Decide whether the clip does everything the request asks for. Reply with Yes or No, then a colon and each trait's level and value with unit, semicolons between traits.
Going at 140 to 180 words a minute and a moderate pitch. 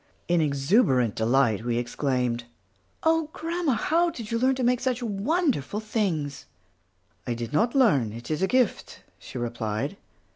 Yes: average, 150 wpm; medium, 175 Hz